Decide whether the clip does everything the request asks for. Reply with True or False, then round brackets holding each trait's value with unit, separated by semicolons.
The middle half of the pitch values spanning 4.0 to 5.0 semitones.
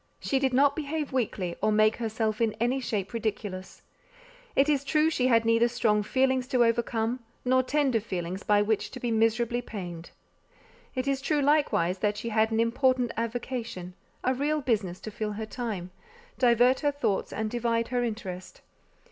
False (3.3 semitones)